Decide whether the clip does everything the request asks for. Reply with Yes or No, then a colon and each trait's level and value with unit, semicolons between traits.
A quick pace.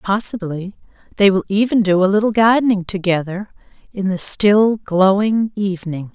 No: slow, 135 wpm